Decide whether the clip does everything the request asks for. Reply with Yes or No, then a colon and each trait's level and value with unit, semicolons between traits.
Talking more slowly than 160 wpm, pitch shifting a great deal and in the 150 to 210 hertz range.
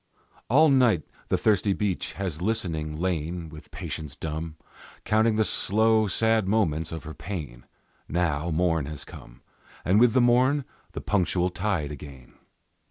No: average, 145 wpm; wide, 5.9 semitones; very low, 90 Hz